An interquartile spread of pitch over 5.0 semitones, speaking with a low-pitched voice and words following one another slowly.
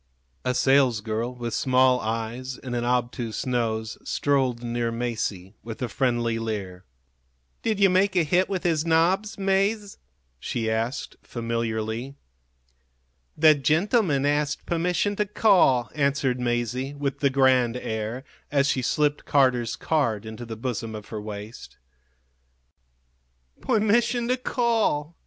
Yes: wide, 5.5 semitones; low, 130 Hz; slow, 130 wpm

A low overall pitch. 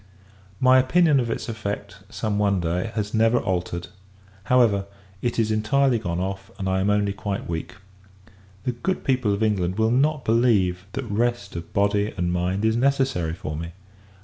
Yes: low, 105 Hz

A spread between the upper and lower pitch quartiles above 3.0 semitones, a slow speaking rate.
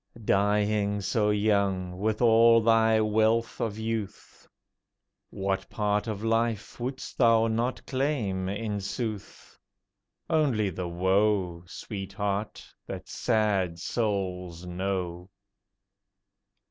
No: average, 2.7 semitones; slow, 95 wpm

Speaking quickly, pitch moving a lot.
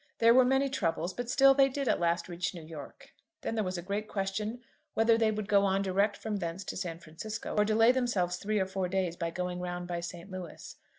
No: fast, 235 wpm; average, 4.0 semitones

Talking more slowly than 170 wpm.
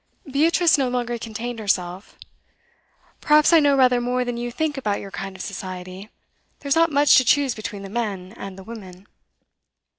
No: average, 175 wpm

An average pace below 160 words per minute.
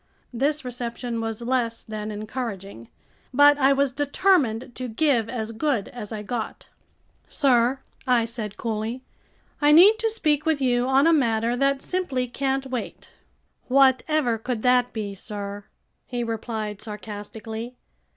Yes: average, 140 wpm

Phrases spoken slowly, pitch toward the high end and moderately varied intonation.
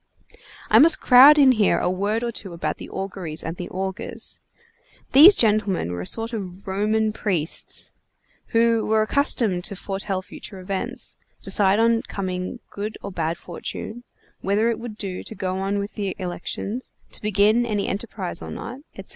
No: average, 170 wpm; high, 205 Hz; average, 3.3 semitones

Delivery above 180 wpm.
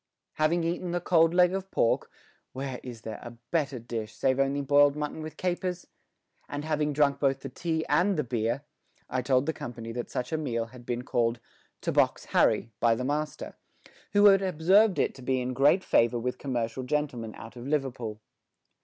Yes: average, 190 wpm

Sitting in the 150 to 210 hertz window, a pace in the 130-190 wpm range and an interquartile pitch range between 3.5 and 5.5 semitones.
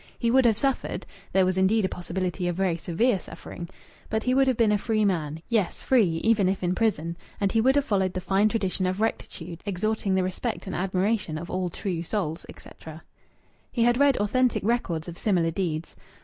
No: high, 190 Hz; fast, 205 wpm; average, 4.1 semitones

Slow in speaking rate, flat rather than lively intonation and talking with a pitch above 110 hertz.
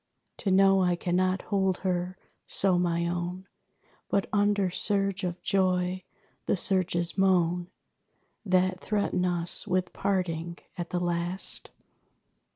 Yes: slow, 120 wpm; narrow, 1.7 semitones; medium, 185 Hz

